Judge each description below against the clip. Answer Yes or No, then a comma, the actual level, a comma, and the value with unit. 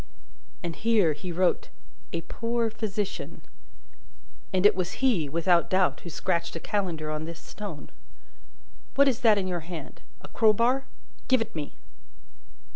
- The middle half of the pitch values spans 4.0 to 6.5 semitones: Yes, average, 4.9 semitones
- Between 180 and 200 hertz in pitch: Yes, medium, 185 Hz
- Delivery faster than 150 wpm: No, average, 145 wpm